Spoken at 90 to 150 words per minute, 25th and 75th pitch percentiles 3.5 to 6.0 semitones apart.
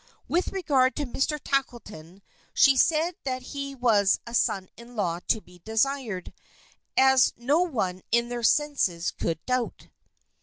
Yes: average, 145 wpm; average, 5.2 semitones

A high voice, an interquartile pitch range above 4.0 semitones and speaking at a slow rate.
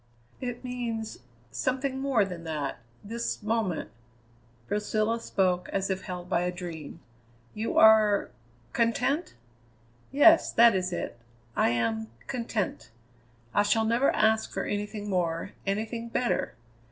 Yes: high, 210 Hz; average, 4.5 semitones; slow, 130 wpm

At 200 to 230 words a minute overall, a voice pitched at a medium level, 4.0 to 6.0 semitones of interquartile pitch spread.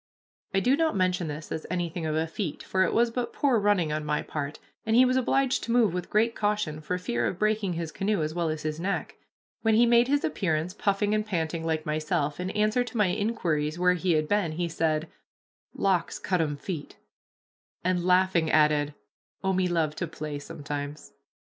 Yes: fast, 205 wpm; medium, 180 Hz; average, 5.1 semitones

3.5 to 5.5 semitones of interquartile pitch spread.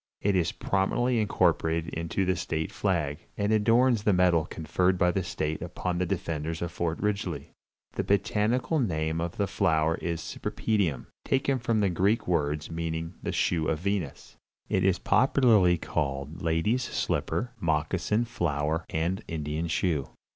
Yes: average, 4.2 semitones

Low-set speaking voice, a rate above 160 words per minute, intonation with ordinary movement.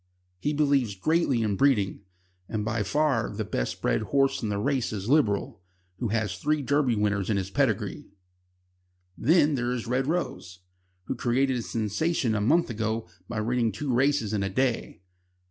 Yes: low, 115 Hz; average, 170 wpm; average, 4.9 semitones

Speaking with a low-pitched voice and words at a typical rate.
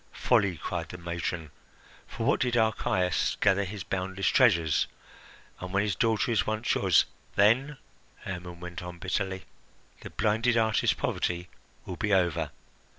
Yes: very low, 95 Hz; average, 150 wpm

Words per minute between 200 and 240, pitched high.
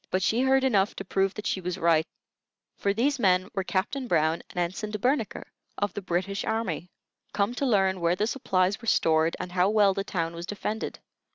Yes: fast, 205 wpm; high, 195 Hz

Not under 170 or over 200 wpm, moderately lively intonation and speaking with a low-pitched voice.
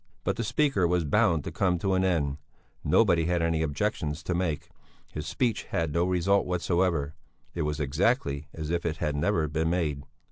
Yes: average, 185 wpm; average, 3.2 semitones; very low, 85 Hz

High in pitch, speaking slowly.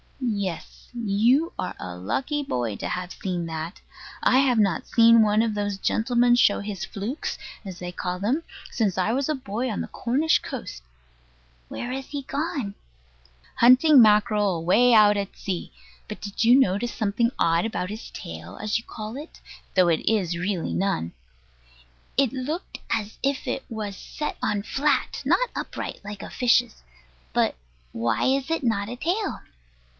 No: high, 215 Hz; average, 170 wpm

